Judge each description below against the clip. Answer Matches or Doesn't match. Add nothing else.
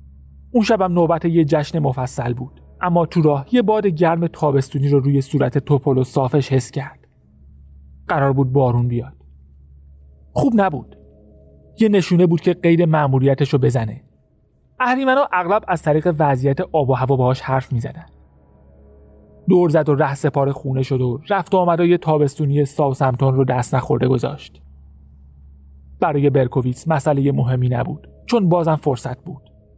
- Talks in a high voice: Doesn't match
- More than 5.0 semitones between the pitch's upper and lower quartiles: Matches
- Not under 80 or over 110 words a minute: Doesn't match